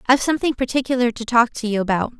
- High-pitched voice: Yes, high, 240 Hz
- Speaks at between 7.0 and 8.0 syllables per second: Yes, 7.1 syllables/s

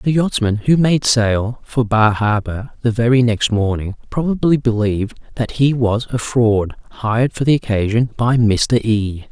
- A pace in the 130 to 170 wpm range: Yes, average, 165 wpm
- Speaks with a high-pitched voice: No, low, 115 Hz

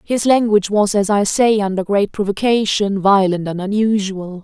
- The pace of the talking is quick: No, average, 160 wpm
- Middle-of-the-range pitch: No, high, 205 Hz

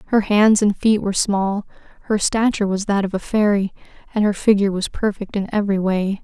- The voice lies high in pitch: Yes, high, 205 Hz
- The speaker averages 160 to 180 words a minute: No, average, 200 wpm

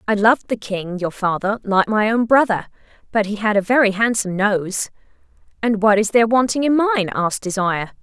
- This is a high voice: Yes, high, 210 Hz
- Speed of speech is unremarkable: Yes, average, 195 wpm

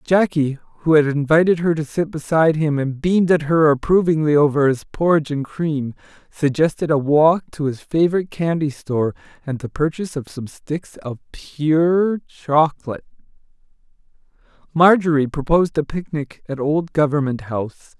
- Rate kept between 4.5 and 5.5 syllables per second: Yes, 5.1 syllables/s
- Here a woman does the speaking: No, male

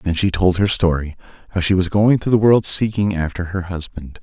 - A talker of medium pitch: No, very low, 95 Hz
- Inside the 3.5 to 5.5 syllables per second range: Yes, 5.3 syllables/s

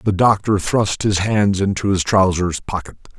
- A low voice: Yes, low, 100 Hz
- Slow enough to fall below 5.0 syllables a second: Yes, 4.4 syllables/s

